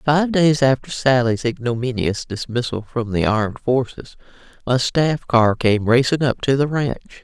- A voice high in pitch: No, low, 125 Hz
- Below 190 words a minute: Yes, average, 160 wpm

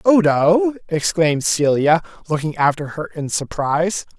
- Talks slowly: Yes, slow, 115 wpm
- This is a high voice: No, medium, 165 Hz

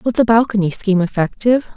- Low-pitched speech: No, high, 210 Hz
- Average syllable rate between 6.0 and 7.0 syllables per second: Yes, 6.7 syllables/s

